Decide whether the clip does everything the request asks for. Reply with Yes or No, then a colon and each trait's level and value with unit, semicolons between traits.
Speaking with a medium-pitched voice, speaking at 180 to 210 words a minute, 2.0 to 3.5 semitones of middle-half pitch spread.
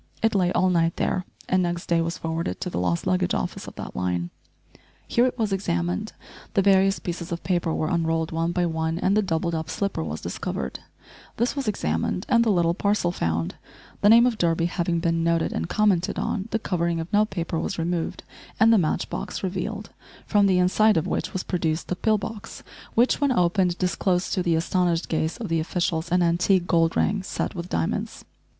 Yes: medium, 175 Hz; fast, 205 wpm; average, 3.0 semitones